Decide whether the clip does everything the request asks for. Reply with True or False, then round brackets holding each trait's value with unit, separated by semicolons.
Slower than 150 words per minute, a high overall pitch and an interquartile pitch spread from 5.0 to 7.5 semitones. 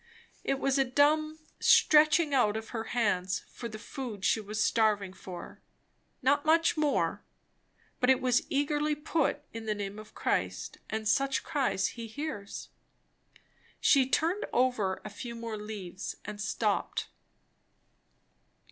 True (140 wpm; 235 Hz; 5.3 semitones)